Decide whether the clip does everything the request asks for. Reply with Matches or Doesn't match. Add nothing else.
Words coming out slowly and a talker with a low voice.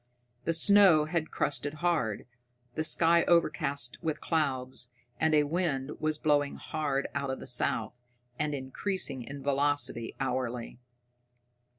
Doesn't match